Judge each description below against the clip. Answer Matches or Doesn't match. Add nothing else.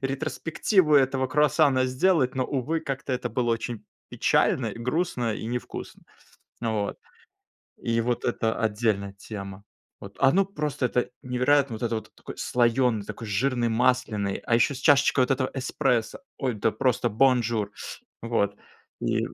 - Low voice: Matches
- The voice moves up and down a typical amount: Matches